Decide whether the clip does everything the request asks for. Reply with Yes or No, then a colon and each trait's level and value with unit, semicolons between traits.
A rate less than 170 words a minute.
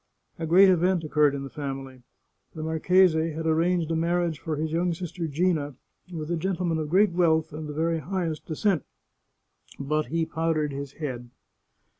No: average, 180 wpm